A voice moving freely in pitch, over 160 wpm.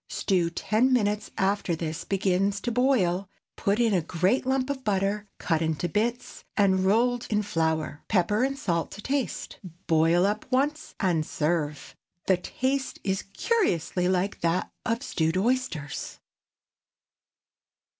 No: wide, 5.8 semitones; slow, 135 wpm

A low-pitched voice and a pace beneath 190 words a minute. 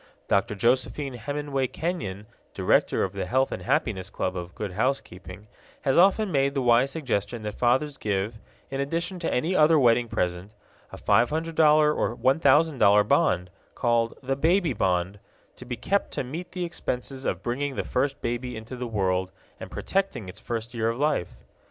Yes: low, 125 Hz; average, 170 wpm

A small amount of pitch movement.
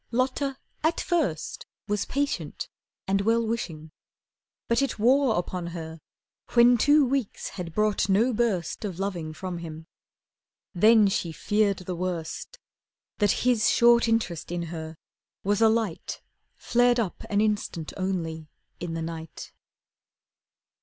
No: wide, 5.6 semitones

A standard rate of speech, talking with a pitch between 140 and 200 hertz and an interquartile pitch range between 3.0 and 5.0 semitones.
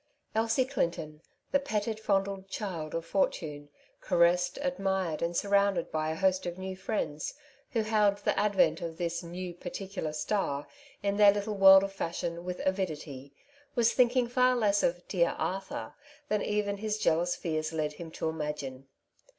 Yes: average, 170 wpm; high, 190 Hz; average, 3.8 semitones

